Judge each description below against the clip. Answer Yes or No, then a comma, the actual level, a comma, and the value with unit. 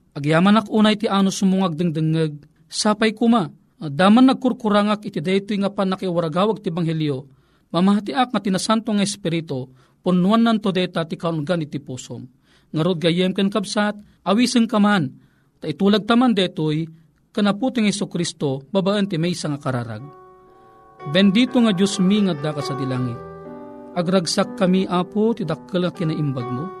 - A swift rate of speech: No, average, 145 wpm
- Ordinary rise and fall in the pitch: Yes, average, 4.6 semitones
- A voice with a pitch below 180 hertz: No, medium, 185 Hz